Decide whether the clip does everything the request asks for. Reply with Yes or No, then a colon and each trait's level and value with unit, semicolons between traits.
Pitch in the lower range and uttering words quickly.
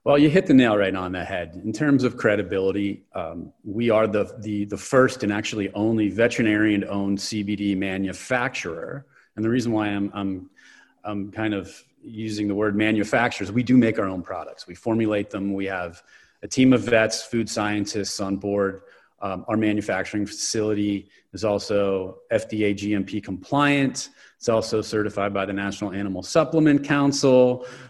No: low, 105 Hz; average, 165 wpm